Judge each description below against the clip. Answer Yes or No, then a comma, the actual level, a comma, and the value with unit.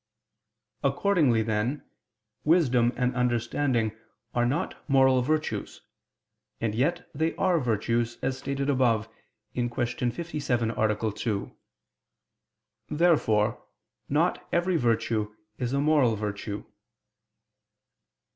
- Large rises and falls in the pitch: No, average, 4.3 semitones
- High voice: No, low, 125 Hz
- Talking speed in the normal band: No, slow, 95 wpm